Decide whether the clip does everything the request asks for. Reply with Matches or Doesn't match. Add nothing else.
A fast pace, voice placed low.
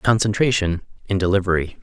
Doesn't match